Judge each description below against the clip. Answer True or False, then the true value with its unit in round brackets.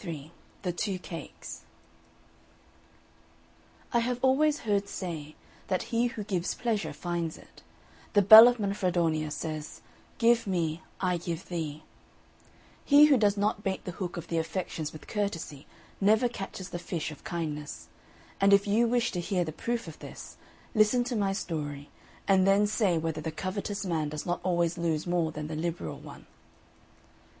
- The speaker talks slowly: False (160 wpm)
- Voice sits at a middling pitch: True (180 Hz)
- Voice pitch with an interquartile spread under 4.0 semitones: False (4.5 semitones)